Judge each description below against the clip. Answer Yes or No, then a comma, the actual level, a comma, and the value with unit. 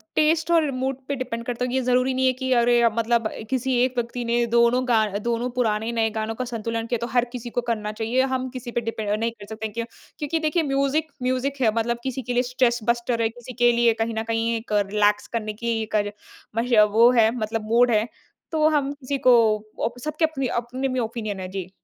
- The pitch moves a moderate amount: No, narrow, 2.3 semitones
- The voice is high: Yes, high, 240 Hz